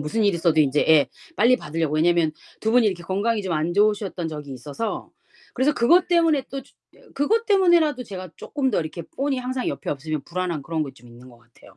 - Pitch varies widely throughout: Yes, wide, 8.5 semitones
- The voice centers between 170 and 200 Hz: Yes, medium, 185 Hz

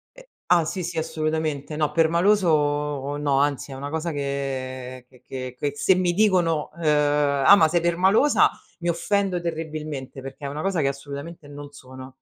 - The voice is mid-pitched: Yes, medium, 150 Hz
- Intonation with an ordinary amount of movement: Yes, average, 3.3 semitones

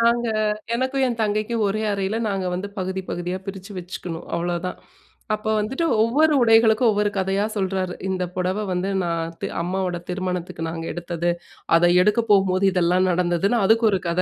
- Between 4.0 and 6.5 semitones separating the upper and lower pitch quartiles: No, average, 3.3 semitones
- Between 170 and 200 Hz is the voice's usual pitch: Yes, high, 190 Hz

